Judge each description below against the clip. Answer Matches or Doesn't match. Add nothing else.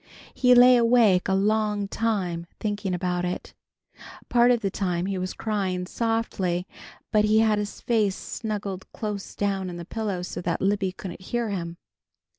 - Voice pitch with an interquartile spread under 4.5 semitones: Matches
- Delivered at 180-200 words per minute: Doesn't match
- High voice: Matches